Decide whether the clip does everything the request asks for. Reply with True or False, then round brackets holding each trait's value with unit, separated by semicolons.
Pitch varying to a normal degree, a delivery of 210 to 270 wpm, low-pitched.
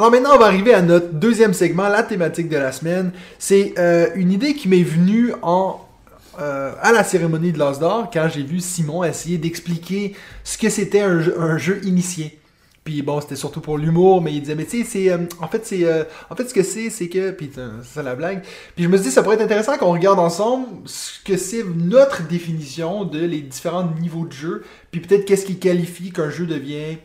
False (3.4 semitones; 220 wpm; 175 Hz)